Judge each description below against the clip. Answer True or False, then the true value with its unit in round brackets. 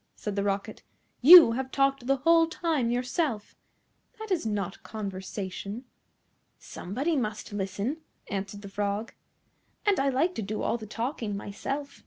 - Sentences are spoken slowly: False (145 wpm)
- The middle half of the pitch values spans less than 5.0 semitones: False (5.4 semitones)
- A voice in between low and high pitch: False (230 Hz)